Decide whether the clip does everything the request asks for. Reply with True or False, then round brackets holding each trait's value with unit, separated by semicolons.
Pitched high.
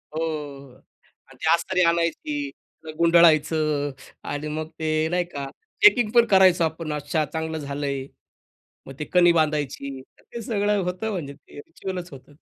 False (160 Hz)